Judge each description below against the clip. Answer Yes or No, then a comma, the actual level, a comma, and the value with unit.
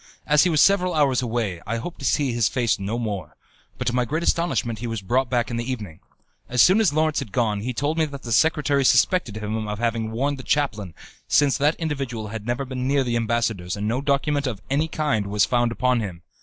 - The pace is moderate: No, fast, 235 wpm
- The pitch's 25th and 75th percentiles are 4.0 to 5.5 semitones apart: Yes, average, 4.5 semitones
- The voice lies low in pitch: Yes, low, 125 Hz